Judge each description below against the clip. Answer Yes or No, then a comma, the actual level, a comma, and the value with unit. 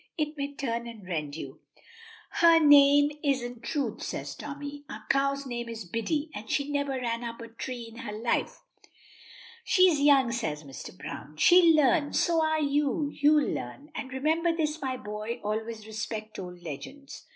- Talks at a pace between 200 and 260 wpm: No, average, 165 wpm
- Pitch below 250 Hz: No, very high, 265 Hz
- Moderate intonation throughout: Yes, average, 4.7 semitones